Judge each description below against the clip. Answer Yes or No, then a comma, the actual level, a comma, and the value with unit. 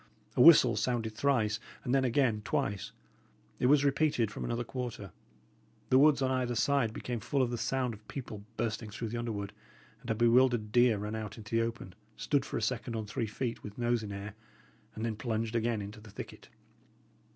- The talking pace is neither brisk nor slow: Yes, average, 195 wpm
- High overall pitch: No, low, 115 Hz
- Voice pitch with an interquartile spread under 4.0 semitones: Yes, average, 2.7 semitones